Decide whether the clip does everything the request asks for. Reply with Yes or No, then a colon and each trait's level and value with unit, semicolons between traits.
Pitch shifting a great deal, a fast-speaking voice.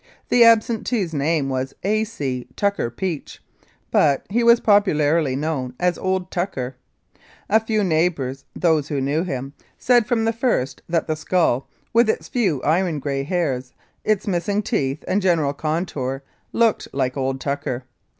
No: wide, 6.8 semitones; average, 155 wpm